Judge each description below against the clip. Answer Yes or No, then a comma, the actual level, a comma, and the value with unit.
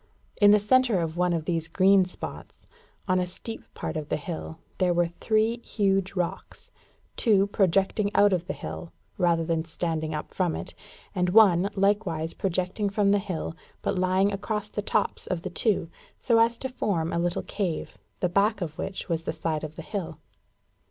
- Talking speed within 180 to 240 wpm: Yes, average, 185 wpm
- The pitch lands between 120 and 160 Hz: No, medium, 185 Hz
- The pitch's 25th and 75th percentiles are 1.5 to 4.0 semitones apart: Yes, average, 3.4 semitones